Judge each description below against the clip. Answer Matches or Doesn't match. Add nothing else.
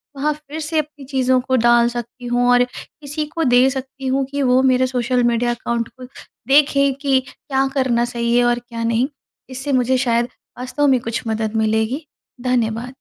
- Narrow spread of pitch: Matches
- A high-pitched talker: Matches